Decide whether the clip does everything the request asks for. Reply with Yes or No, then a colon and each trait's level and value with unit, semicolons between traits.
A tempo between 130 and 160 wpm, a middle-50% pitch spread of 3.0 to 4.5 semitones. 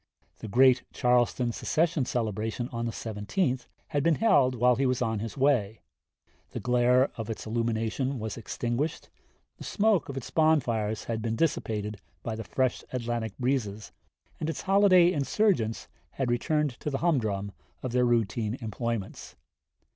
Yes: average, 150 wpm; average, 3.6 semitones